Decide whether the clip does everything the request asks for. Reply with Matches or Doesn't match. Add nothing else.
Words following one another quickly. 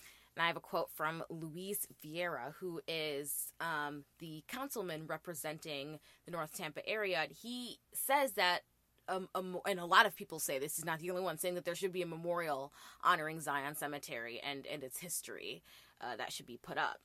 Doesn't match